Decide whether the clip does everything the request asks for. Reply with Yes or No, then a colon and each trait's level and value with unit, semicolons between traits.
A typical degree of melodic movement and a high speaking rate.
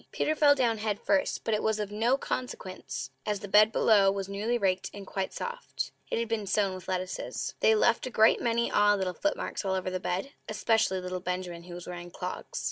Yes: average, 3.5 semitones; fast, 215 wpm